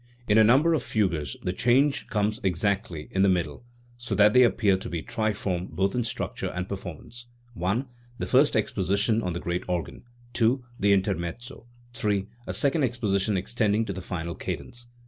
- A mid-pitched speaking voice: No, low, 105 Hz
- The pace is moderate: Yes, average, 175 wpm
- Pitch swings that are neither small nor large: Yes, average, 4.3 semitones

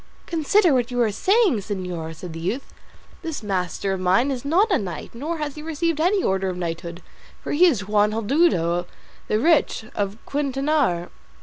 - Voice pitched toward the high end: Yes, high, 230 Hz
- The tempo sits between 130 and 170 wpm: No, average, 180 wpm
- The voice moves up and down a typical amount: No, wide, 8.9 semitones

